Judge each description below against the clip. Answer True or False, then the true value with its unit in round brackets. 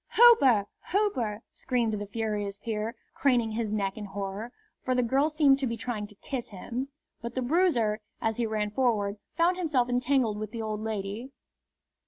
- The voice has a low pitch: False (230 Hz)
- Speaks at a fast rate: False (175 wpm)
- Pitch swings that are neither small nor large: True (3.7 semitones)